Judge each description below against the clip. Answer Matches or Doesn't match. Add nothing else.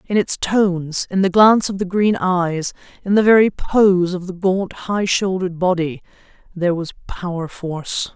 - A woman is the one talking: Matches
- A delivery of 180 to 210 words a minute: Doesn't match